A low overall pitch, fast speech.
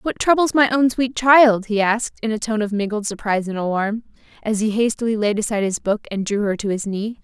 No: high, 220 Hz; fast, 240 wpm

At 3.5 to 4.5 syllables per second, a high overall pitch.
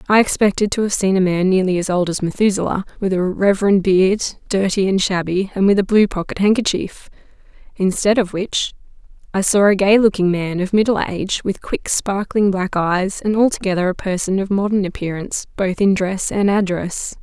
No: 5.3 syllables/s; high, 195 Hz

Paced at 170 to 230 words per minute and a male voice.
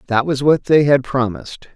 Yes: fast, 205 wpm; male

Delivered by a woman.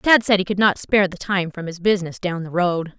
Yes: female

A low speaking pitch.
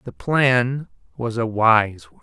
Yes: low, 120 Hz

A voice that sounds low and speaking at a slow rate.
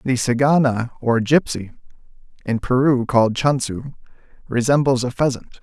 Yes: low, 125 Hz; slow, 115 wpm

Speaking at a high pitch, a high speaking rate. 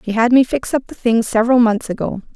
Yes: high, 230 Hz; fast, 255 wpm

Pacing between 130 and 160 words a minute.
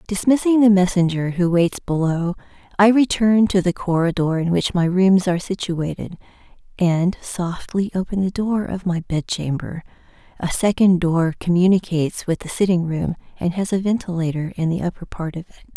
No: average, 170 wpm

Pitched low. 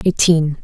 No: medium, 165 Hz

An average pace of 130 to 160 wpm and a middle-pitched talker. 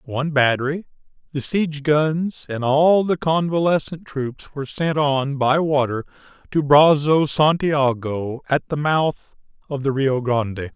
Yes: average, 140 wpm; medium, 145 Hz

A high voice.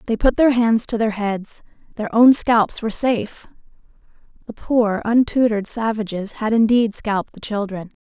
Yes: high, 220 Hz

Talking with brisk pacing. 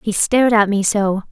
Yes: fast, 230 wpm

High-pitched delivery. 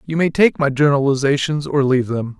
No: medium, 140 Hz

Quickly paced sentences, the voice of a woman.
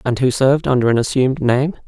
No: fast, 225 wpm; male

